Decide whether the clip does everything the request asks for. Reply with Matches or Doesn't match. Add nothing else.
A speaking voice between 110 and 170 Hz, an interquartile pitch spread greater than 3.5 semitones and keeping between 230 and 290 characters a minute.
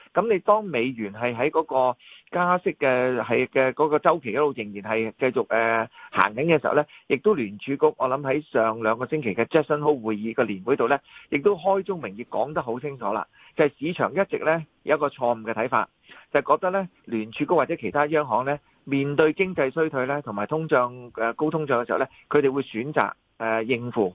Doesn't match